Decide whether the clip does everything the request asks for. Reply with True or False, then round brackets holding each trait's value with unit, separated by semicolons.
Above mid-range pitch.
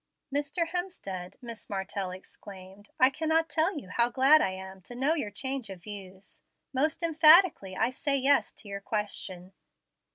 True (235 Hz)